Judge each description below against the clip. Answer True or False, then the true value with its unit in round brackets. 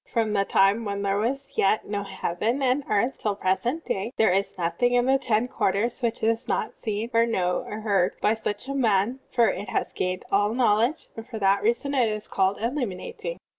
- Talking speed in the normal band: False (210 wpm)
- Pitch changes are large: False (3.4 semitones)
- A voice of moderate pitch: False (220 Hz)